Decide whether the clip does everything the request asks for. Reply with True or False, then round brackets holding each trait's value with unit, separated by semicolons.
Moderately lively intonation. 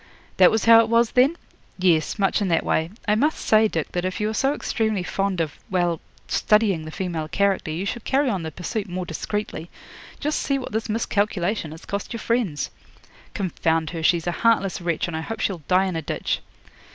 True (4.7 semitones)